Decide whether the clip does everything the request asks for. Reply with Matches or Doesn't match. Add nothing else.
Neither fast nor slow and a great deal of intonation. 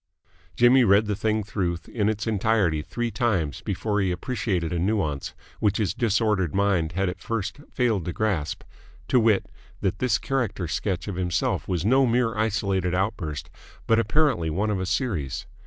Doesn't match